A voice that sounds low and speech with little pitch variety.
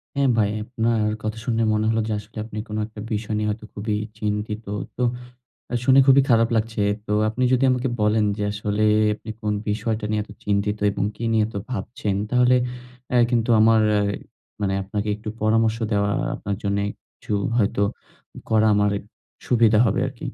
Yes: low, 110 Hz; narrow, 1.6 semitones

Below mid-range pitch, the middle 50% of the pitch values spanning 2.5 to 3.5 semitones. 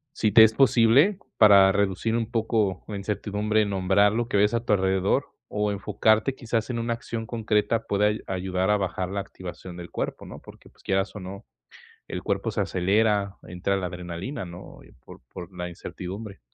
Yes: low, 100 Hz; average, 2.8 semitones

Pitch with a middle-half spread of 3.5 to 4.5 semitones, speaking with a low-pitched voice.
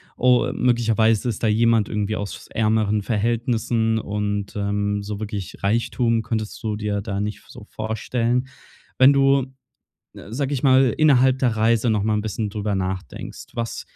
No: narrow, 2.4 semitones; low, 110 Hz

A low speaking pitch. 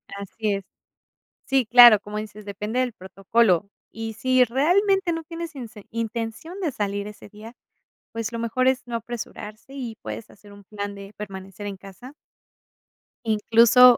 No: high, 225 Hz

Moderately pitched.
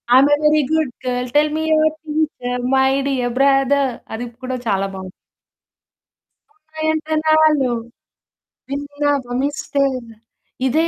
No: very high, 280 Hz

